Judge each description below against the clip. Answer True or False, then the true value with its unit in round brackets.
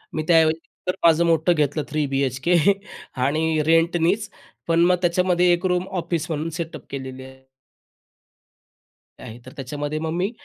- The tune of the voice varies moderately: True (3.0 semitones)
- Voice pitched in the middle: True (160 Hz)